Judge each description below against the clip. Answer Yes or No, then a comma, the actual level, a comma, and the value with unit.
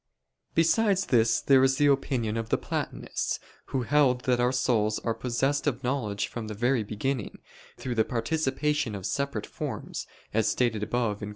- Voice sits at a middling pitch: No, low, 125 Hz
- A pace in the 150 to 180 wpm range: Yes, average, 170 wpm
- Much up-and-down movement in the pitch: No, average, 3.7 semitones